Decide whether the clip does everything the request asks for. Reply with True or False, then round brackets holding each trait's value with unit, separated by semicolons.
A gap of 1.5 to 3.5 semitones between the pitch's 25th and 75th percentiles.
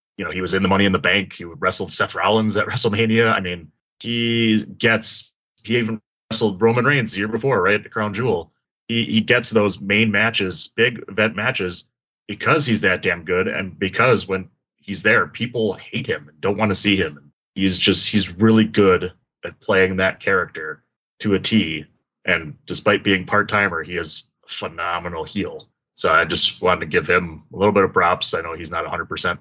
True (2.9 semitones)